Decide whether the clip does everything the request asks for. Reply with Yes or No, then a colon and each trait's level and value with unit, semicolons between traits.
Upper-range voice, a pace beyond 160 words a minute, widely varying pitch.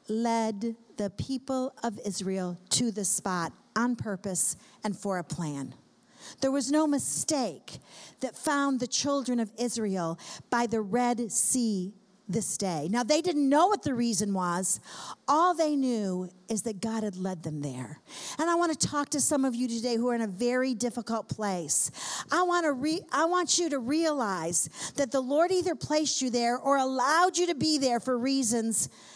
Yes: high, 240 Hz; average, 185 wpm; wide, 5.8 semitones